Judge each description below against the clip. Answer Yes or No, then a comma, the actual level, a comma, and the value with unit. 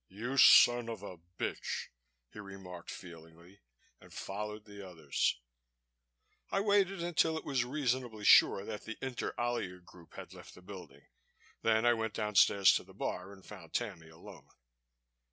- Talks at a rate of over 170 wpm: No, average, 155 wpm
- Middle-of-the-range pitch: No, low, 105 Hz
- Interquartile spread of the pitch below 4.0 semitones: No, average, 4.9 semitones